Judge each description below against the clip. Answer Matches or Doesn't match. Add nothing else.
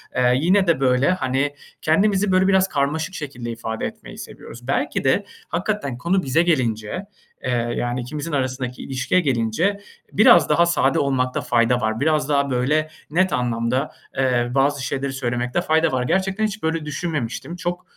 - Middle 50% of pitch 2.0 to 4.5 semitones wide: Doesn't match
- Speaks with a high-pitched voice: Doesn't match